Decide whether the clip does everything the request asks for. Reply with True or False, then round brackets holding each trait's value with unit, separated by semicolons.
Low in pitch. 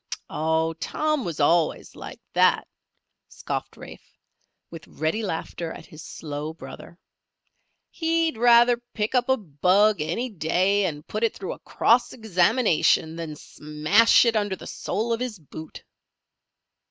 False (190 Hz)